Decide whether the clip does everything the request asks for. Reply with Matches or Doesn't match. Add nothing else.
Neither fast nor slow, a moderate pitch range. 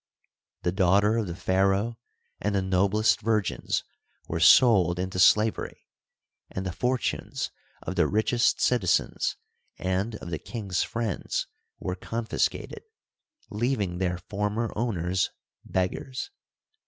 Doesn't match